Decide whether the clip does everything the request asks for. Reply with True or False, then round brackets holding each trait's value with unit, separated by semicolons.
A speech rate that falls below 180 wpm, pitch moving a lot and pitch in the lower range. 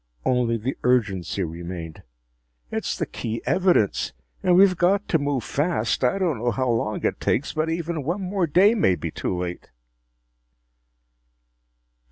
True (150 wpm; 8.6 semitones; 130 Hz)